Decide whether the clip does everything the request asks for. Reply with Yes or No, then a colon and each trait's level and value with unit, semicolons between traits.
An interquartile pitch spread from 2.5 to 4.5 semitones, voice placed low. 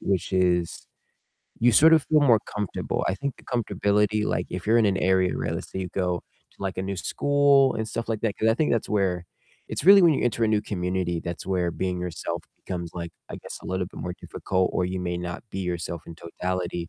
Yes: average, 4.1 semitones; very low, 95 Hz